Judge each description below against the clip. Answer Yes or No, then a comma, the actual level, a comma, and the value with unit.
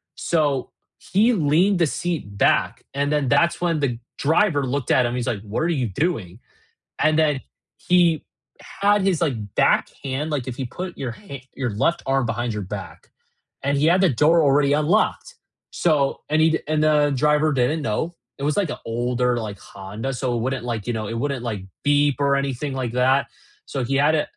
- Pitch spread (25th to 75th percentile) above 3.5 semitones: Yes, average, 4.2 semitones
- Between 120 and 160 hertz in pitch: Yes, medium, 140 Hz